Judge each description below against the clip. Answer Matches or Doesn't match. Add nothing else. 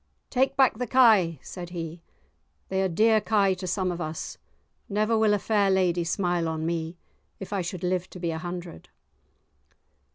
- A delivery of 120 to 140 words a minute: Doesn't match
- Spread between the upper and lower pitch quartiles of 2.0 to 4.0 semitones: Matches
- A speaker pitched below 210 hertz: Matches